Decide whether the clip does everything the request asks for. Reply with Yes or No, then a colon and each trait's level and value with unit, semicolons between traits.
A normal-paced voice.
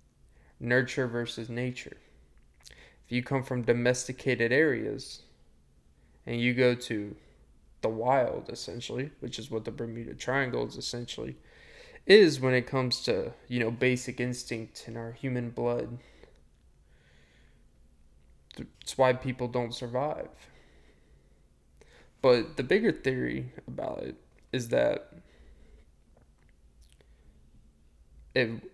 No: slow, 105 wpm